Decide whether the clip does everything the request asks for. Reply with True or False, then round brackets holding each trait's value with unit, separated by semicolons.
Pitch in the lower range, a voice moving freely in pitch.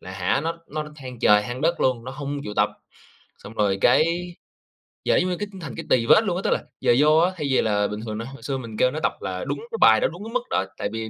True (130 Hz; 6.2 semitones)